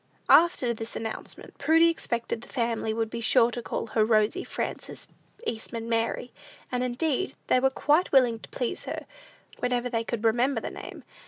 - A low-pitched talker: No, high, 235 Hz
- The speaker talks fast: No, average, 170 wpm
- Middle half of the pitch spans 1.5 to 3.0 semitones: Yes, narrow, 2.4 semitones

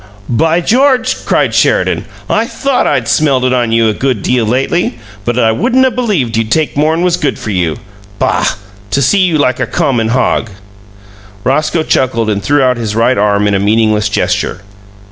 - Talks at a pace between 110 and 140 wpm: No, average, 185 wpm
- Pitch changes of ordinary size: No, wide, 6.3 semitones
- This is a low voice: Yes, low, 125 Hz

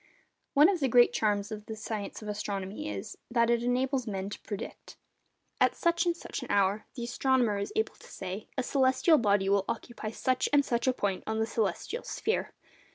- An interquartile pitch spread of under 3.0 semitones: No, average, 4.3 semitones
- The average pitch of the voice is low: No, high, 225 Hz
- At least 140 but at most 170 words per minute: No, average, 200 wpm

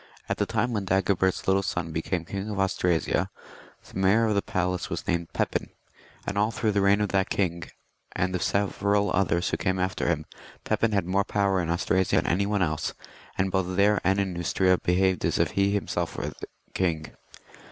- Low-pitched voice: Yes, very low, 95 Hz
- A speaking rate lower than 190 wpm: No, average, 200 wpm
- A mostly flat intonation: Yes, narrow, 2.0 semitones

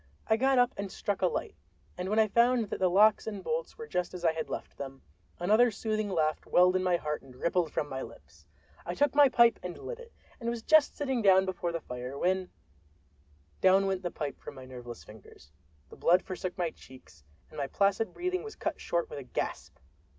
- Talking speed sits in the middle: No, fast, 220 wpm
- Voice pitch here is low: No, medium, 185 Hz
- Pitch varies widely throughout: Yes, wide, 7.1 semitones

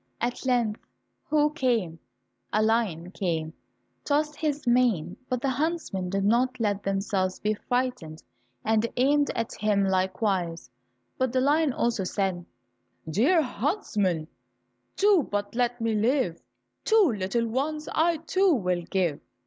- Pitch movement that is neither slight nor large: No, wide, 5.9 semitones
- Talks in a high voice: Yes, high, 230 Hz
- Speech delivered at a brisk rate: No, slow, 135 wpm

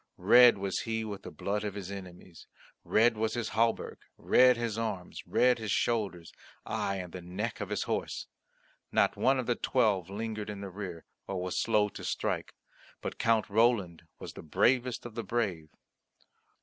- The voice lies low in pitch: Yes, low, 105 Hz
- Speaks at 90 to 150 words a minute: No, average, 175 wpm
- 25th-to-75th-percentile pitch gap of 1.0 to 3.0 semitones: No, average, 3.4 semitones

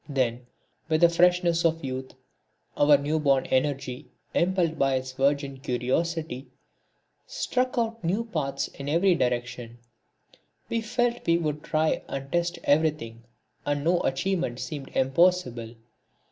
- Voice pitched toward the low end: No, medium, 150 Hz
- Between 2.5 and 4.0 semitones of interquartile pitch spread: No, average, 4.6 semitones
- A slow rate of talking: Yes, slow, 130 wpm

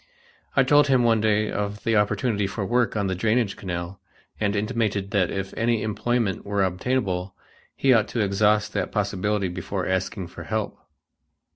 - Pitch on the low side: Yes, low, 105 Hz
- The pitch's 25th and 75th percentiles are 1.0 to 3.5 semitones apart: Yes, average, 2.7 semitones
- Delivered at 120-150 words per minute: No, average, 165 wpm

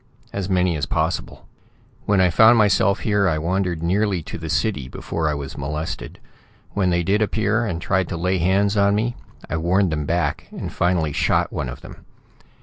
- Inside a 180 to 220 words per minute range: Yes, average, 190 wpm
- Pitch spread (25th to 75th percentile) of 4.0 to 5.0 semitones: No, average, 3.6 semitones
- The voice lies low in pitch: Yes, very low, 90 Hz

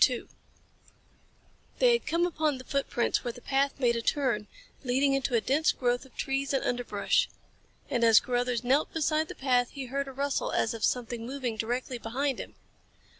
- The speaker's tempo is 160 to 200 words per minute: Yes, average, 175 wpm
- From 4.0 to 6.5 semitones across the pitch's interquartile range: No, narrow, 2.5 semitones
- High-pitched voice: Yes, very high, 260 Hz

